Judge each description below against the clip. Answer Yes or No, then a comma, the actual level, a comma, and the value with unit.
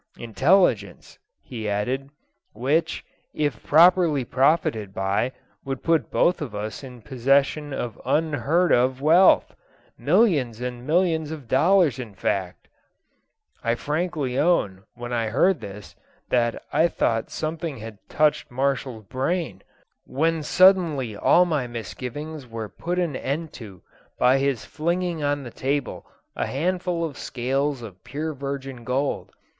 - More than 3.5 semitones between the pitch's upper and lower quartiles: Yes, average, 5.0 semitones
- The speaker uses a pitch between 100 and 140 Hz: Yes, low, 135 Hz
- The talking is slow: Yes, slow, 130 wpm